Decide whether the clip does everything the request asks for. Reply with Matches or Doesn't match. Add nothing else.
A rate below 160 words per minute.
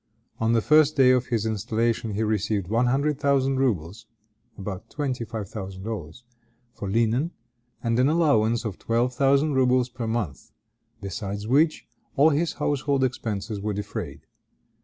Matches